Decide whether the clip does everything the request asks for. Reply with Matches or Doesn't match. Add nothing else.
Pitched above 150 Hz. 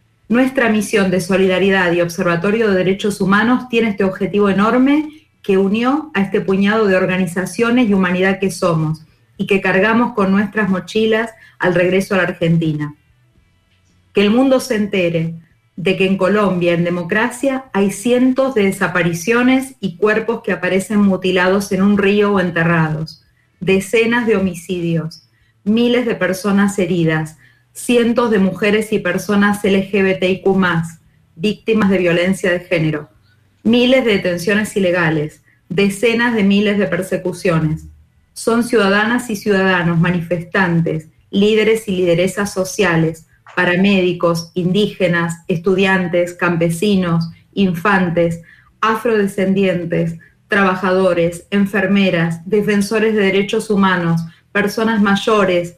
Matches